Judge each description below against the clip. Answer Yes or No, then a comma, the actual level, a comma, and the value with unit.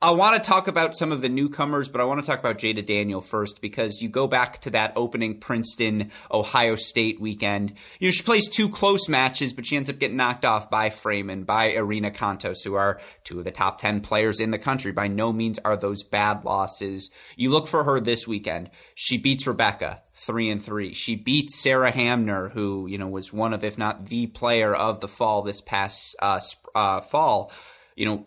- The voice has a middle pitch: No, low, 110 Hz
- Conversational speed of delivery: No, fast, 215 wpm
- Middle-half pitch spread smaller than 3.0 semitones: No, average, 4.0 semitones